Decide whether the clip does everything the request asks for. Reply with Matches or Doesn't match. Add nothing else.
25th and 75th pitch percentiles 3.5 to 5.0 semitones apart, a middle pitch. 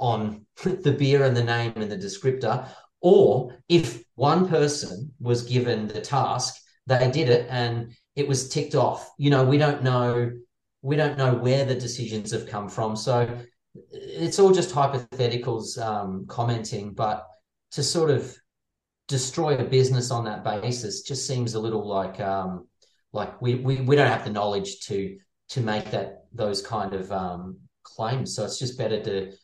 Doesn't match